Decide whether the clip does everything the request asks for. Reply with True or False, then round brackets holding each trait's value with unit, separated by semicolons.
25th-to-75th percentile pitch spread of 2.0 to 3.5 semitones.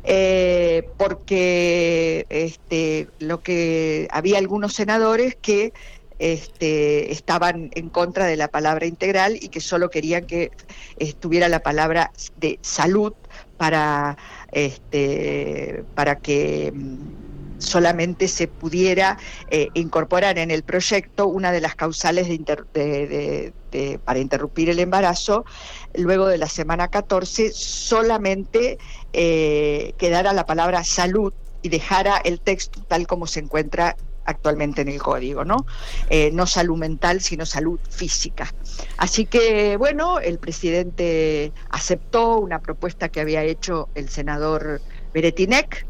True (3.2 semitones)